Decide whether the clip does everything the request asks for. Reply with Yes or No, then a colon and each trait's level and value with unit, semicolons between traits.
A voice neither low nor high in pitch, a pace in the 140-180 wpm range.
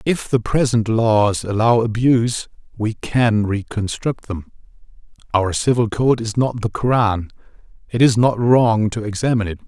No: low, 110 Hz; average, 150 wpm